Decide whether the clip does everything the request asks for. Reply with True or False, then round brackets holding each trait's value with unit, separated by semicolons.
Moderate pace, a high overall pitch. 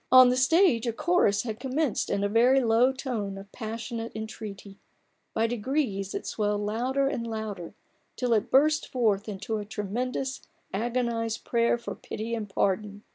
True (160 wpm; 230 Hz)